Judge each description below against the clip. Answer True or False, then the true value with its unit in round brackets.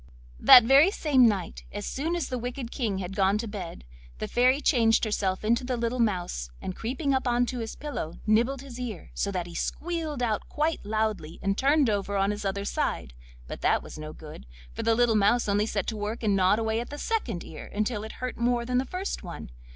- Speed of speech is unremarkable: False (225 wpm)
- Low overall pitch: False (225 Hz)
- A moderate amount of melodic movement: True (4.1 semitones)